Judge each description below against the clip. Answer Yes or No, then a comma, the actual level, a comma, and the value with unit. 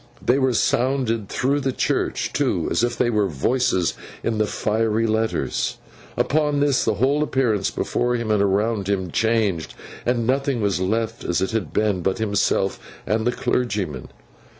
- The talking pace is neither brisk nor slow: Yes, average, 165 wpm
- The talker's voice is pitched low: Yes, low, 110 Hz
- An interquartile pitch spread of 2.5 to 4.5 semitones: Yes, average, 3.7 semitones